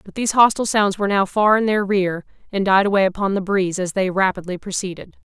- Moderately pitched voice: No, high, 195 Hz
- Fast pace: Yes, fast, 225 wpm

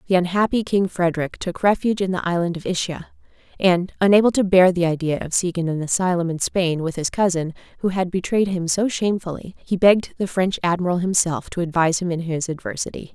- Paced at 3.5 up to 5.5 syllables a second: No, 6.0 syllables/s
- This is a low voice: No, medium, 180 Hz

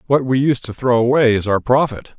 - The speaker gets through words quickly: Yes, fast, 245 wpm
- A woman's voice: No, male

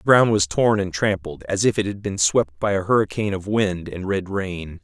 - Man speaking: Yes, male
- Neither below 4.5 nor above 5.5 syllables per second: Yes, 5.1 syllables/s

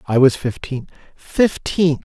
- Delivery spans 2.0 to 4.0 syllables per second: Yes, 3.7 syllables/s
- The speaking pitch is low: No, medium, 145 Hz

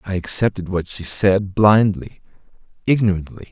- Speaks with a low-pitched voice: Yes, very low, 95 Hz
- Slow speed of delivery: Yes, slow, 120 wpm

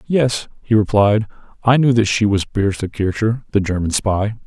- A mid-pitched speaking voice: No, low, 105 Hz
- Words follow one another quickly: No, average, 175 wpm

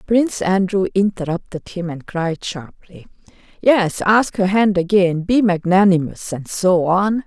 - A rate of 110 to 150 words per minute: Yes, average, 140 wpm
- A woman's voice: Yes, female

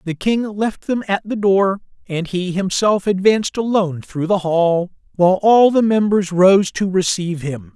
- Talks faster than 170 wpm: Yes, average, 180 wpm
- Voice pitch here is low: No, high, 190 Hz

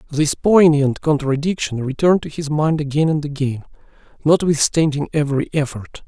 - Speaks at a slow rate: Yes, slow, 130 wpm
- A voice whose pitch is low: No, medium, 150 Hz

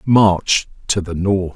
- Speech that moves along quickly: No, average, 155 wpm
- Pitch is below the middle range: Yes, very low, 95 Hz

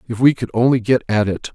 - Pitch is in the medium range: No, low, 115 Hz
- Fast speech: Yes, fast, 270 wpm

